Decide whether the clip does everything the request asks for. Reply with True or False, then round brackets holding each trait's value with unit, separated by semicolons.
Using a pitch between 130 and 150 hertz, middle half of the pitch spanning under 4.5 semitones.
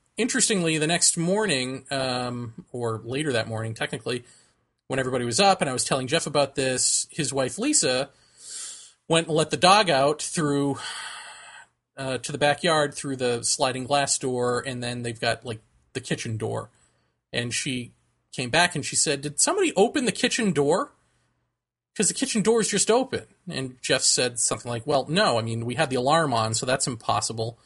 False (140 Hz; 5.2 semitones)